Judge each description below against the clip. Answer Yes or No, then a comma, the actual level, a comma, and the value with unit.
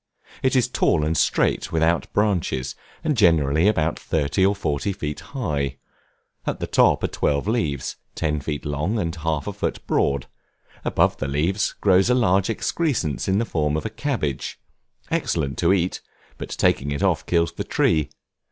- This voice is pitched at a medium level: No, very low, 85 Hz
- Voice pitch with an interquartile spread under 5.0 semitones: No, wide, 5.5 semitones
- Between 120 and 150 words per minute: No, average, 170 wpm